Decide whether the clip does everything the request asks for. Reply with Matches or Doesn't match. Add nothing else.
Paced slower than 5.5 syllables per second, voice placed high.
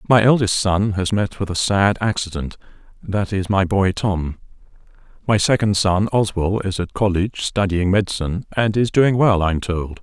Doesn't match